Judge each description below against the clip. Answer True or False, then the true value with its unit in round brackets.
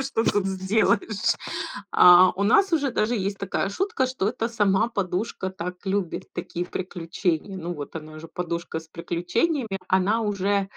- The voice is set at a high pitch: True (195 Hz)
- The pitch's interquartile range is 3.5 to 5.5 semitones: True (3.8 semitones)